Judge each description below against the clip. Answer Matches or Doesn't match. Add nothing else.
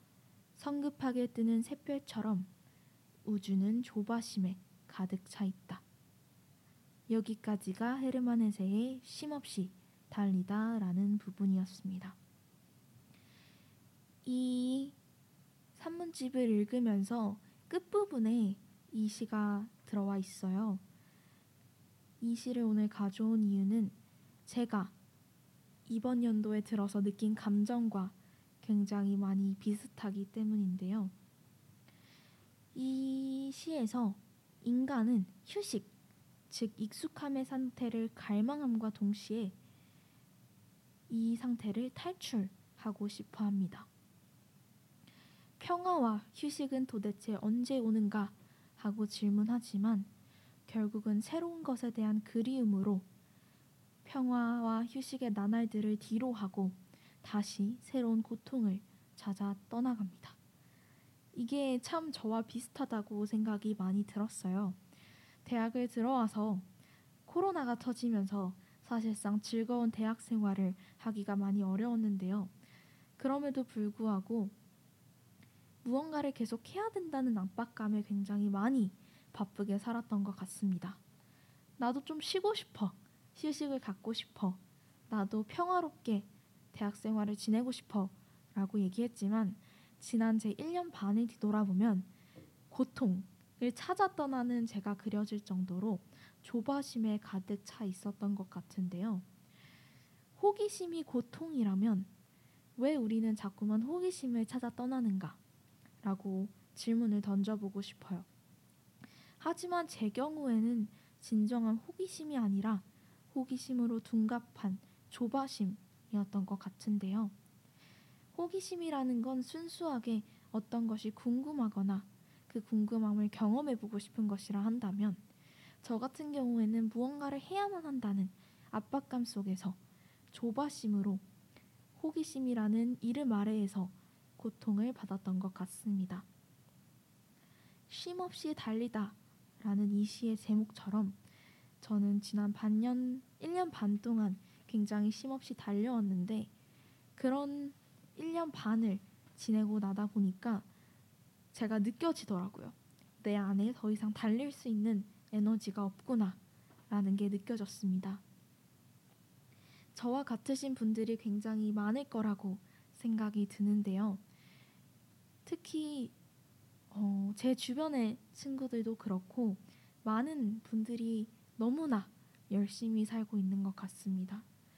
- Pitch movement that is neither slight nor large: Matches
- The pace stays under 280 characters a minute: Matches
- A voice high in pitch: Matches